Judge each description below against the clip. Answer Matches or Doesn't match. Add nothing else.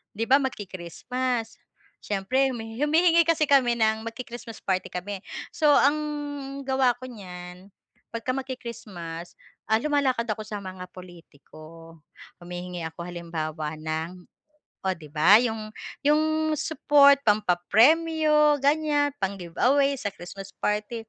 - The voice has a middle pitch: Doesn't match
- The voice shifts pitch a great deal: Matches